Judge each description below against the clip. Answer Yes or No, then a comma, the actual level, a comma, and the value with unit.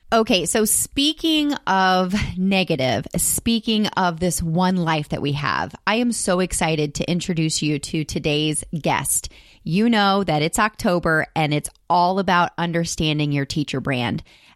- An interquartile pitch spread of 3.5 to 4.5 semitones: Yes, average, 4.1 semitones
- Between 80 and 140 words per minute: No, average, 150 wpm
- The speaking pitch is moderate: Yes, medium, 175 Hz